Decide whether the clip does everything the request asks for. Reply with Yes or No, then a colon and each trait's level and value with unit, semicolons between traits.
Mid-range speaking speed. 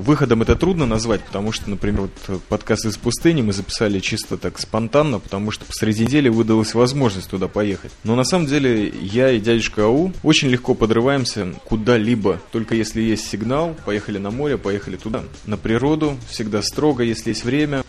No: fast, 175 wpm